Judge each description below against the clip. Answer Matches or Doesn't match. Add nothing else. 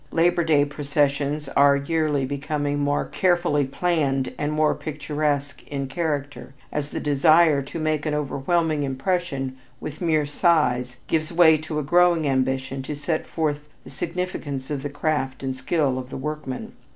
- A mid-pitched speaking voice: Matches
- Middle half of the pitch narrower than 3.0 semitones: Matches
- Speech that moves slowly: Doesn't match